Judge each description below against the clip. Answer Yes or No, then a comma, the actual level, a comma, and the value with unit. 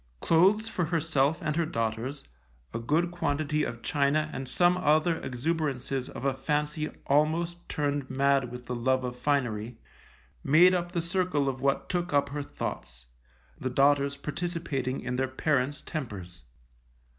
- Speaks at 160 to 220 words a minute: No, average, 150 wpm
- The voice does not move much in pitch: No, average, 3.9 semitones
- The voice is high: No, medium, 145 Hz